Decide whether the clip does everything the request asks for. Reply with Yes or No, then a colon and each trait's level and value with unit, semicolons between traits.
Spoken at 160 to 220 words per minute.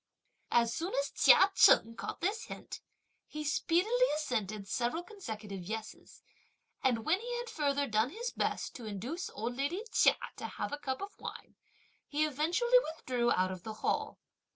Yes: average, 165 wpm